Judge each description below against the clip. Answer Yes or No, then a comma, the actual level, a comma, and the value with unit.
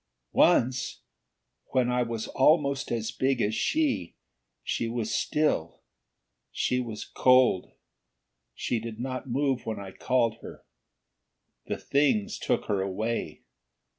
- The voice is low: Yes, low, 120 Hz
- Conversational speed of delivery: No, slow, 120 wpm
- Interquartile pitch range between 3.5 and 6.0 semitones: No, average, 3.1 semitones